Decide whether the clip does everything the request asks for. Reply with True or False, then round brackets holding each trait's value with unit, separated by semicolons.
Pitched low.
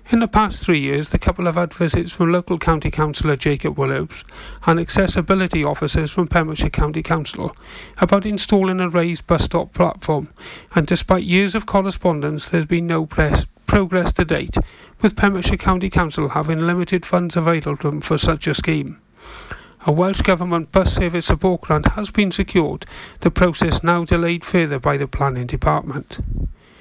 False (170 Hz)